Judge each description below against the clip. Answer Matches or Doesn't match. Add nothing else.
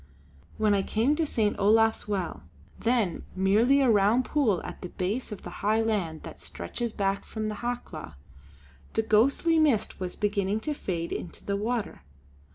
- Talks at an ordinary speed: Matches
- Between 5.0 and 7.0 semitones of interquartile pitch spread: Doesn't match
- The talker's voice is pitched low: Doesn't match